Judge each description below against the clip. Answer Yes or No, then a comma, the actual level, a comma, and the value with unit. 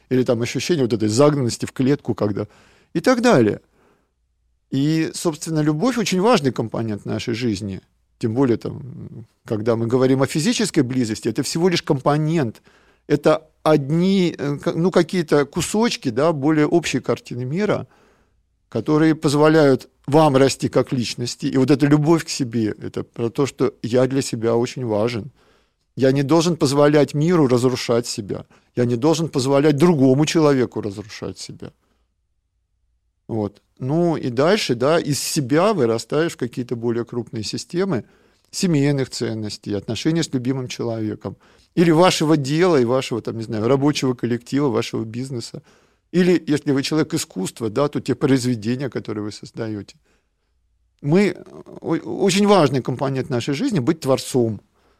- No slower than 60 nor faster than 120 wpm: No, average, 140 wpm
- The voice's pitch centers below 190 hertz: Yes, low, 135 Hz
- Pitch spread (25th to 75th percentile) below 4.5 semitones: No, average, 5.2 semitones